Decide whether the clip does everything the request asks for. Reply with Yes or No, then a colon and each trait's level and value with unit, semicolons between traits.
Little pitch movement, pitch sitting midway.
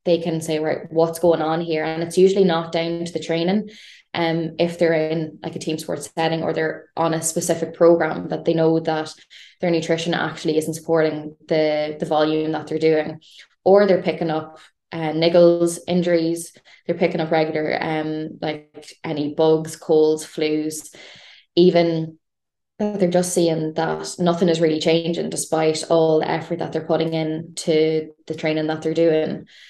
Yes: narrow, 1.3 semitones; medium, 160 Hz